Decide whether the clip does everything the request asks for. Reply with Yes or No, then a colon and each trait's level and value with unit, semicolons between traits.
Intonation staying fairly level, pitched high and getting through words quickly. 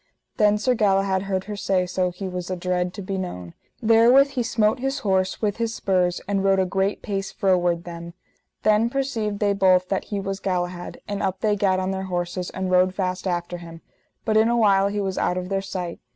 Yes: narrow, 2.3 semitones; high, 195 Hz; fast, 215 wpm